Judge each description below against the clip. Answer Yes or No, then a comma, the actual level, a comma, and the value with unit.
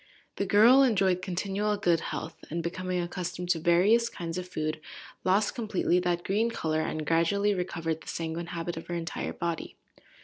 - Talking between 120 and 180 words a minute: Yes, average, 170 wpm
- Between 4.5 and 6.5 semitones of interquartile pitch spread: No, average, 3.1 semitones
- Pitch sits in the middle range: Yes, medium, 175 Hz